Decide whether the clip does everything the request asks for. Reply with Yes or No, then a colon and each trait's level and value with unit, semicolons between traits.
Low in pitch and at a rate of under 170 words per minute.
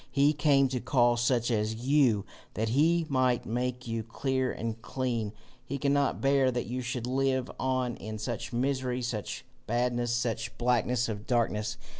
Yes: low, 125 Hz; average, 160 wpm